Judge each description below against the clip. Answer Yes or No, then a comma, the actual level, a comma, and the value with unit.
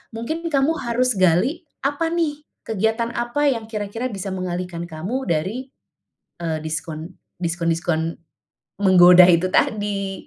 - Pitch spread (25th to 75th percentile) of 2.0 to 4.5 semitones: No, wide, 5.6 semitones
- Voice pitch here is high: Yes, high, 195 Hz